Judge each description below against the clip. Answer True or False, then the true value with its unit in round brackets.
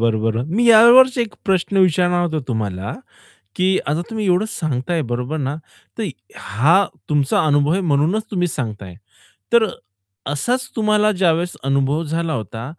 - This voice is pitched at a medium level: True (165 Hz)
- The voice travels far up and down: True (6.2 semitones)